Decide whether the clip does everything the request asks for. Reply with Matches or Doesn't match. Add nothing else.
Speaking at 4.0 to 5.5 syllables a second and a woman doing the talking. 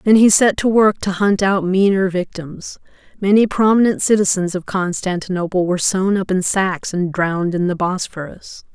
Matches